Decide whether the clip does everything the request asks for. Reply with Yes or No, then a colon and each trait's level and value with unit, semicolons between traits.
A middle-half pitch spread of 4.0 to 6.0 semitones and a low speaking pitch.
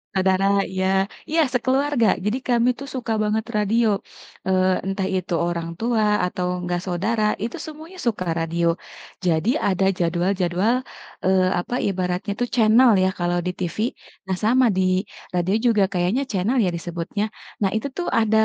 No: average, 4.3 semitones; high, 195 Hz